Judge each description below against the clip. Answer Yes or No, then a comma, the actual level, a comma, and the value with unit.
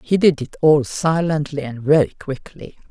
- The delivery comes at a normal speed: Yes, average, 165 wpm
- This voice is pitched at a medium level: Yes, medium, 150 Hz